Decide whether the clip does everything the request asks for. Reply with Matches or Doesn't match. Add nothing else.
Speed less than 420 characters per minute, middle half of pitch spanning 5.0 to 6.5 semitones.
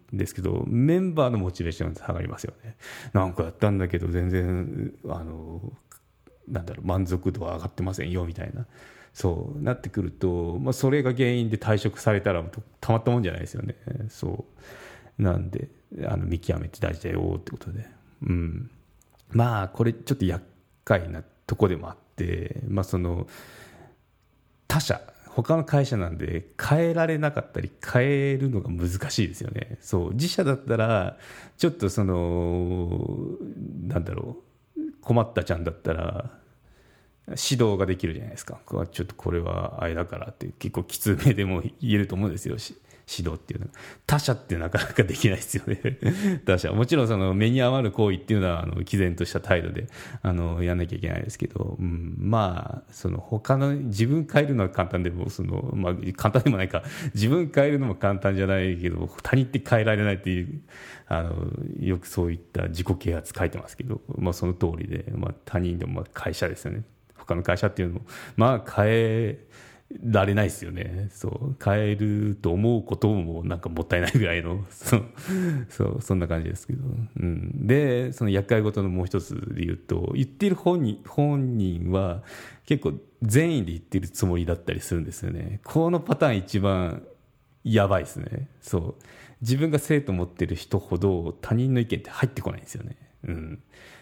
Matches